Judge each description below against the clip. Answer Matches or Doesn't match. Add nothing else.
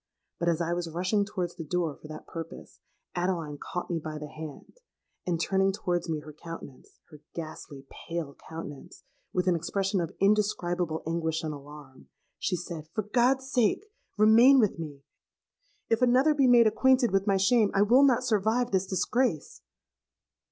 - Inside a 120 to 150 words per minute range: Doesn't match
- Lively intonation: Doesn't match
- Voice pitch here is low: Doesn't match